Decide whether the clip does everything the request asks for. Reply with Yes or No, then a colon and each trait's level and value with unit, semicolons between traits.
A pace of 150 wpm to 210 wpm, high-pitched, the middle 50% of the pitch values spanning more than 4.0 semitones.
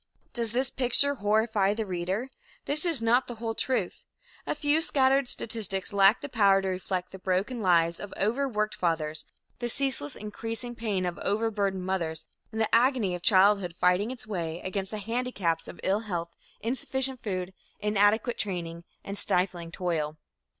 Yes: average, 160 wpm; high, 205 Hz; average, 4.5 semitones